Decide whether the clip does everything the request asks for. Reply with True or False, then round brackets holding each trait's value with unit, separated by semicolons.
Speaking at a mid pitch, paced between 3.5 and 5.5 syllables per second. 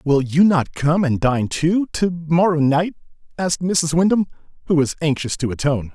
True (160 Hz; 4.9 syllables/s)